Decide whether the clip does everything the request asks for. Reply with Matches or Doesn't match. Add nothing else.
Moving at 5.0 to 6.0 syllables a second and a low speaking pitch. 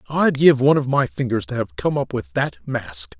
Matches